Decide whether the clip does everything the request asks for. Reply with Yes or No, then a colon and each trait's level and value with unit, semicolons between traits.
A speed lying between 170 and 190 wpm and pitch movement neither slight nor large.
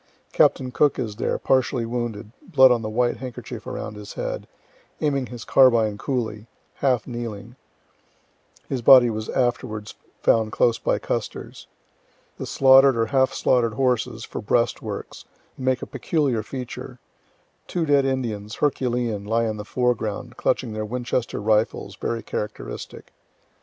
No: slow, 135 wpm; average, 3.1 semitones